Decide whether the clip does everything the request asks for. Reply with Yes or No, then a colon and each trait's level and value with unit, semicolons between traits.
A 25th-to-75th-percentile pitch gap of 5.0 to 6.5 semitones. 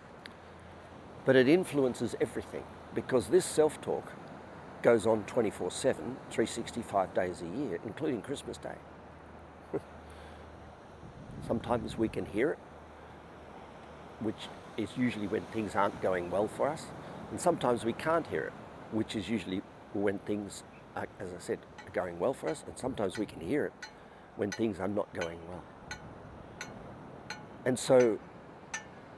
Yes: wide, 5.5 semitones